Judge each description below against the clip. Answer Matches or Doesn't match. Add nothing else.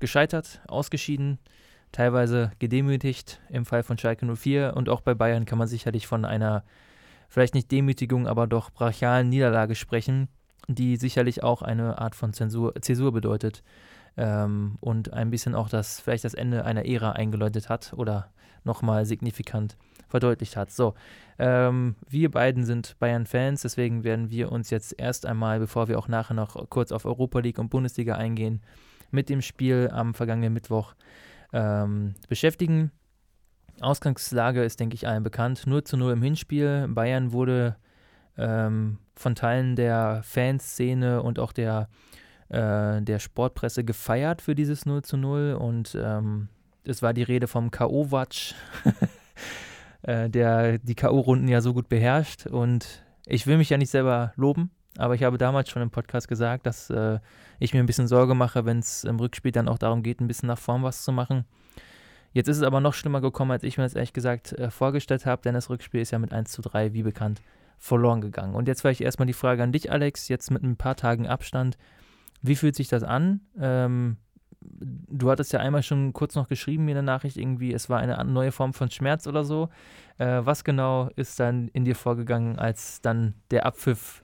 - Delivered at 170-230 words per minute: Matches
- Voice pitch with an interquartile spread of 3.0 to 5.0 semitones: Doesn't match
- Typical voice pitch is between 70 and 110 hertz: Doesn't match